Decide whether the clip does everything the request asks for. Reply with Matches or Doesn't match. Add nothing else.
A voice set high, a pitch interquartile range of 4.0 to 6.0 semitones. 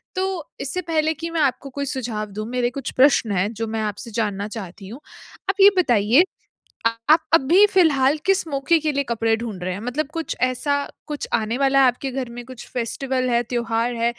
Matches